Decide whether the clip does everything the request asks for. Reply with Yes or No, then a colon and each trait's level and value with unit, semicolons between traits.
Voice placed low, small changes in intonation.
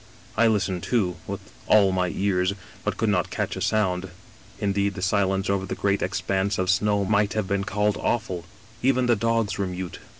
Yes: low, 100 Hz; narrow, 2.0 semitones